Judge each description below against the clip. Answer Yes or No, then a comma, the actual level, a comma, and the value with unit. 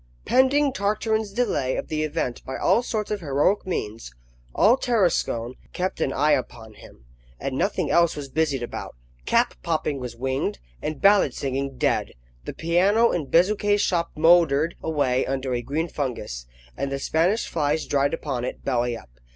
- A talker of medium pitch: Yes, medium, 150 Hz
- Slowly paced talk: No, average, 165 wpm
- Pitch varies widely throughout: Yes, wide, 6.2 semitones